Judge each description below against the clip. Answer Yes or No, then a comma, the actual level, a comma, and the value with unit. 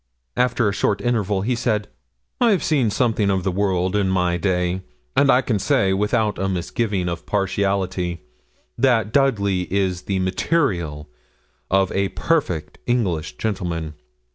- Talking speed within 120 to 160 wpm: Yes, average, 140 wpm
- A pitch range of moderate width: Yes, average, 3.9 semitones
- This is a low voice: Yes, low, 100 Hz